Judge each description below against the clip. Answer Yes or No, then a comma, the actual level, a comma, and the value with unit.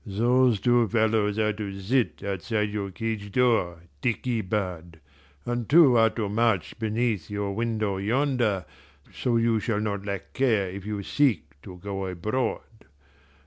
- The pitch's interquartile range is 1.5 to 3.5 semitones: Yes, average, 3.0 semitones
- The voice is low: Yes, low, 105 Hz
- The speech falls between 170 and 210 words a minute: No, average, 145 wpm